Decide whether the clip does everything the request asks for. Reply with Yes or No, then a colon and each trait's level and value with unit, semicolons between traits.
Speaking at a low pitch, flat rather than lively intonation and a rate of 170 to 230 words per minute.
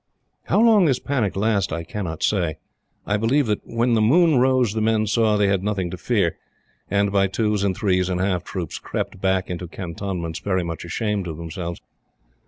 No: low, 100 Hz; average, 3.7 semitones; average, 190 wpm